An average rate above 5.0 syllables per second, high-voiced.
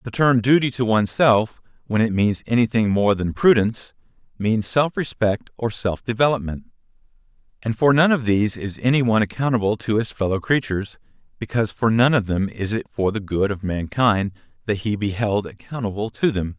No: 5.5 syllables/s; low, 110 Hz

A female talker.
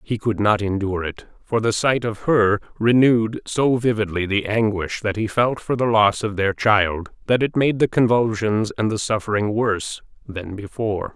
No: male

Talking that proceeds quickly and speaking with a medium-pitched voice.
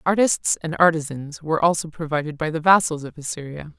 No: average, 175 wpm; medium, 160 Hz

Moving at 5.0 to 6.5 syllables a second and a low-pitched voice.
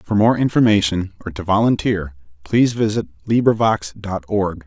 Yes: 5.1 syllables/s; low, 100 Hz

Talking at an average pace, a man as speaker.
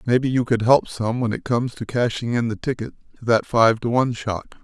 No: fast, 245 wpm; male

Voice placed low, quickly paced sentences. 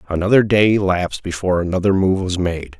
No: very low, 90 Hz; average, 170 wpm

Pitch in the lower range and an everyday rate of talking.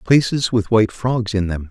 No: low, 110 Hz; fast, 210 wpm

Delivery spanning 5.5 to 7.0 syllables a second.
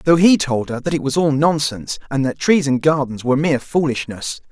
Yes: 5.7 syllables/s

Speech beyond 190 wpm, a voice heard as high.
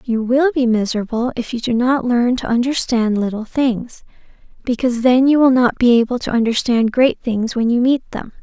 Yes: average, 200 wpm; high, 240 Hz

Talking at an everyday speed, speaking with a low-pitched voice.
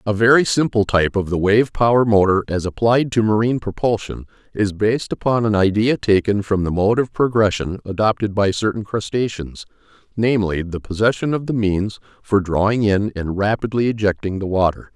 Yes: average, 175 wpm; low, 105 Hz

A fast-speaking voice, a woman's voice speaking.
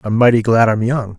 No: fast, 255 wpm; male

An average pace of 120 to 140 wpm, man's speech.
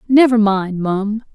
No: slow, 135 wpm; female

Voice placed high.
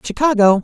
Yes: high, 235 Hz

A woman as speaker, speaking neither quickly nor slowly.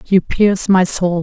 Yes: female; average, 195 wpm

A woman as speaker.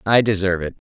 No: male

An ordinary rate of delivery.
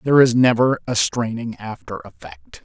Yes: average, 160 wpm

